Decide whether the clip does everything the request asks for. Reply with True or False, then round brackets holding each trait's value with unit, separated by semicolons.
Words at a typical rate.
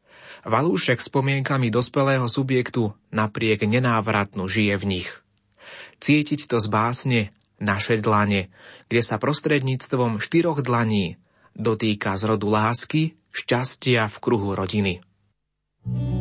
False (105 wpm)